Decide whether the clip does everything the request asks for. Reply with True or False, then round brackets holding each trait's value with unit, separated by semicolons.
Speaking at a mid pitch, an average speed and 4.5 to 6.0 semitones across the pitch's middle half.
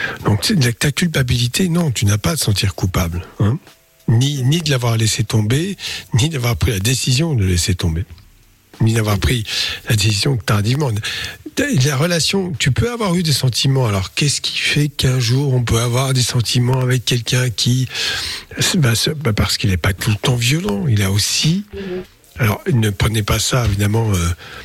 False (125 Hz; 180 wpm; 4.9 semitones)